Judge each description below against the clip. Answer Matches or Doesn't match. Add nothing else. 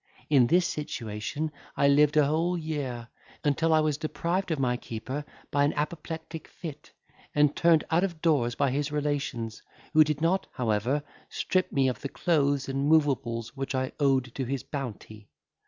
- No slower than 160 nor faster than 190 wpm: Matches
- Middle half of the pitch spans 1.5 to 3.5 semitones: Matches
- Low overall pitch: Doesn't match